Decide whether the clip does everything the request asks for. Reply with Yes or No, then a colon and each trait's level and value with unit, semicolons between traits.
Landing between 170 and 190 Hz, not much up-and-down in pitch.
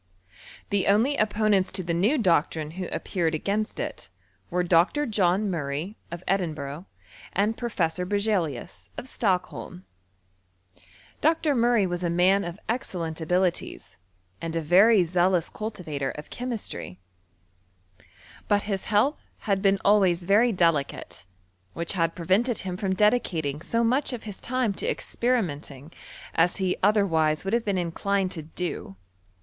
No: medium, 185 Hz; average, 4.2 semitones